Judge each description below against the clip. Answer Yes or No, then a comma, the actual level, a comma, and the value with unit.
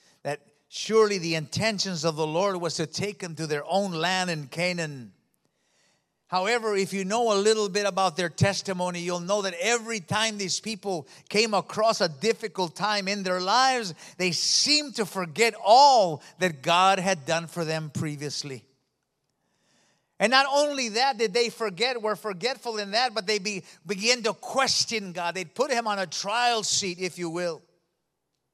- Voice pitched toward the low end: No, high, 195 Hz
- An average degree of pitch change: Yes, average, 4.3 semitones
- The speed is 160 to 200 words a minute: Yes, average, 170 wpm